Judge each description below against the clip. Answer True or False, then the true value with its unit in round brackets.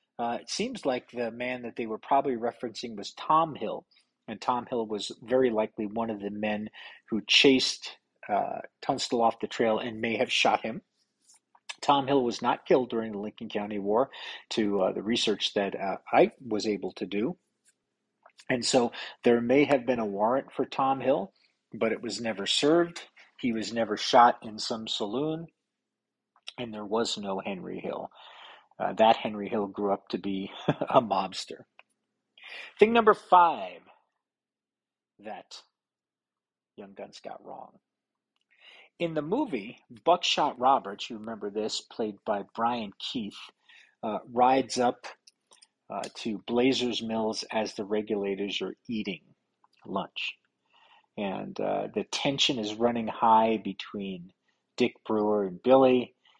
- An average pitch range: True (3.4 semitones)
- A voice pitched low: True (115 Hz)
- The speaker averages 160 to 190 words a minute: False (150 wpm)